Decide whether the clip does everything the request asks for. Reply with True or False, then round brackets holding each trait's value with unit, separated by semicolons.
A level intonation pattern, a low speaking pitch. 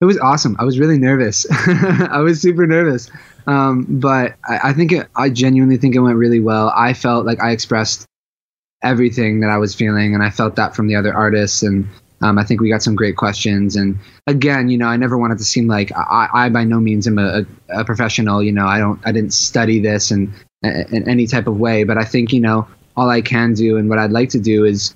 False (3.0 semitones; 115 Hz)